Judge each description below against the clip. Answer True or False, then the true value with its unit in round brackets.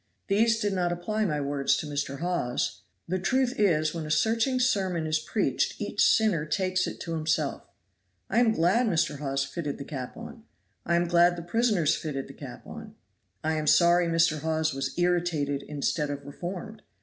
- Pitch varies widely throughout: False (4.3 semitones)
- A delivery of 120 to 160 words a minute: False (185 wpm)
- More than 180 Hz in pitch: False (170 Hz)